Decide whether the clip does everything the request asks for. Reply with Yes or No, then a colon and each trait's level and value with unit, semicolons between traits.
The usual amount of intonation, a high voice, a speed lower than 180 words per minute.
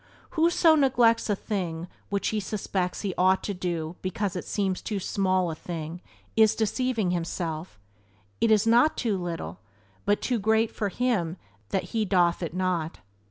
Yes: average, 3.9 semitones; high, 195 Hz; average, 165 wpm